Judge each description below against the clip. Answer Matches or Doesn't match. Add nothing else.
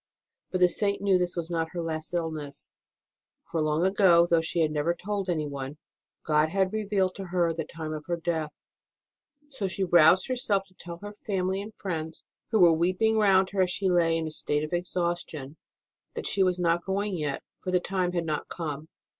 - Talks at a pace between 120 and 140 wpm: Doesn't match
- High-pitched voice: Doesn't match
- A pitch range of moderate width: Matches